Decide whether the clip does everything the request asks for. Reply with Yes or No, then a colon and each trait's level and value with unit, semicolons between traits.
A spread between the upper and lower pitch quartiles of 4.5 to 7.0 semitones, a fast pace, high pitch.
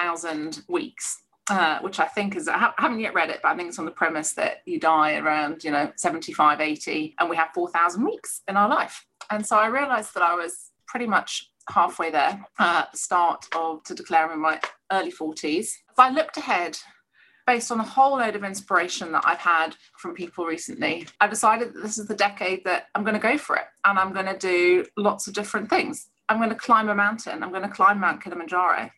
Yes: average, 4.9 semitones; fast, 230 wpm; high, 195 Hz